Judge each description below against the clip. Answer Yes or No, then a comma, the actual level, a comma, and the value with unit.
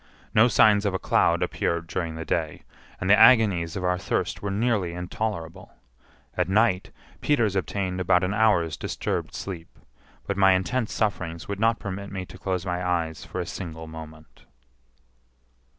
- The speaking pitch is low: Yes, very low, 95 Hz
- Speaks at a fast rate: No, average, 165 wpm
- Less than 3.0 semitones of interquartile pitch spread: No, average, 3.4 semitones